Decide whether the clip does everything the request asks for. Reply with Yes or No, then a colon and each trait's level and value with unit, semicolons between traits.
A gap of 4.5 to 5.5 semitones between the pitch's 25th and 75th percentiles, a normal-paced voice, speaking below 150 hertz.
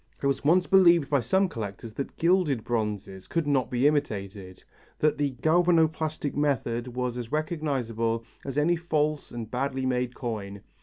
Yes: average, 5.0 semitones; average, 155 wpm; low, 135 Hz